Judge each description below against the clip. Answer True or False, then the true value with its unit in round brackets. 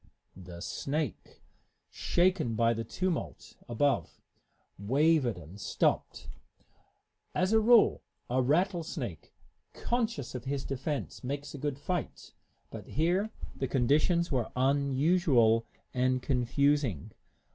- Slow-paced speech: True (105 wpm)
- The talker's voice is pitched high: False (140 Hz)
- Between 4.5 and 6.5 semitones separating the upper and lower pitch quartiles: True (5.2 semitones)